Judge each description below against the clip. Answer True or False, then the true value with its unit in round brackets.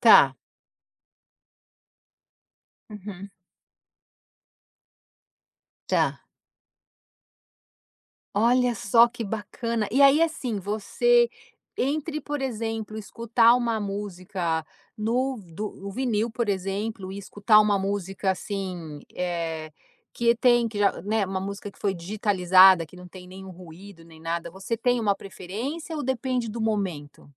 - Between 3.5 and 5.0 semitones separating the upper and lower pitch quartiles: True (3.8 semitones)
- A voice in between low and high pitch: False (205 Hz)